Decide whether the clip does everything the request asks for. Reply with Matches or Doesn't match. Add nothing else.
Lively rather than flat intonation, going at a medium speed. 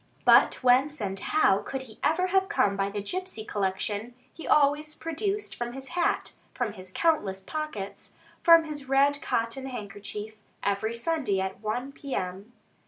Matches